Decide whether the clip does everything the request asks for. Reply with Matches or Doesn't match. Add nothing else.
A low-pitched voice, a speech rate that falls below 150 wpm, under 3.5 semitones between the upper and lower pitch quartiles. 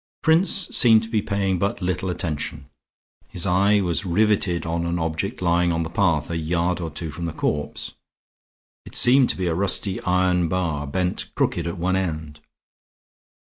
Doesn't match